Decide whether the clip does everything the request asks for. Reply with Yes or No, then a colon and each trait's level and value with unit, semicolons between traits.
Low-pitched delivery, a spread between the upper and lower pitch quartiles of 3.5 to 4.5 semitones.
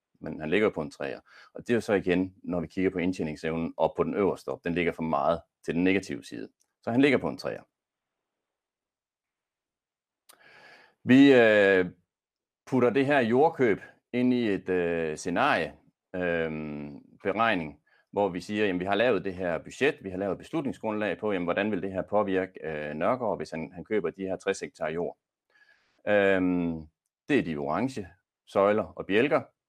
Yes: very low, 95 Hz; average, 4.0 semitones